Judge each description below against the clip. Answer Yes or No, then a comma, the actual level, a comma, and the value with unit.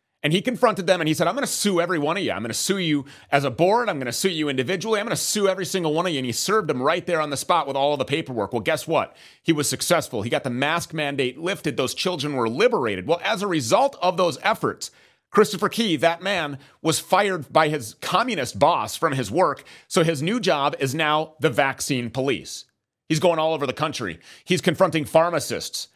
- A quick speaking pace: Yes, fast, 235 wpm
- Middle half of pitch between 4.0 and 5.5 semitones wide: Yes, average, 4.6 semitones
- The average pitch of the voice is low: No, medium, 160 Hz